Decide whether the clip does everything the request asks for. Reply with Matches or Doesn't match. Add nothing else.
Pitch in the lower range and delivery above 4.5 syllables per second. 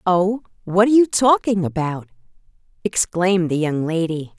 Doesn't match